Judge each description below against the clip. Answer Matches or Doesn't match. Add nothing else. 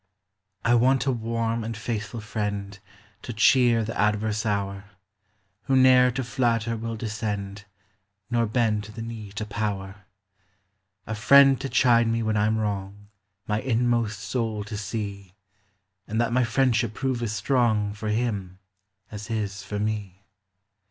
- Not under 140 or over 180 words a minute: Matches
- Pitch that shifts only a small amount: Matches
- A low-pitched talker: Matches